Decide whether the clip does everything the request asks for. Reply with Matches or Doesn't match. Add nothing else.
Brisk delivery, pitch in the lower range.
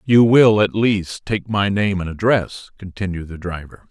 Doesn't match